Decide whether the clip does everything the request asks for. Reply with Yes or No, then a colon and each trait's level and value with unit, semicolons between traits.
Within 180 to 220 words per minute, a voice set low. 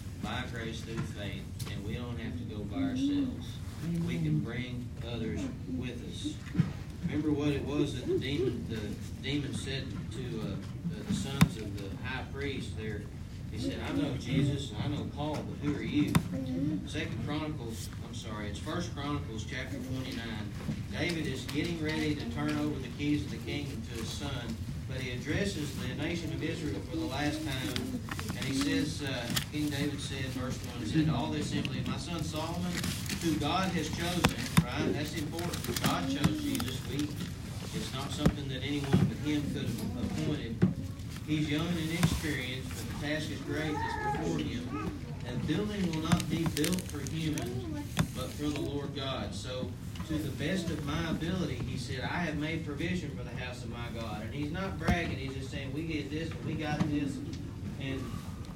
Yes: average, 185 wpm; low, 130 Hz